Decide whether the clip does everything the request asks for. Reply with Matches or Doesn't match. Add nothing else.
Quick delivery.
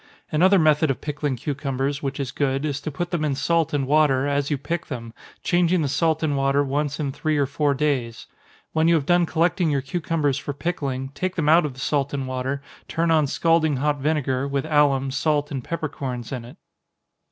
Matches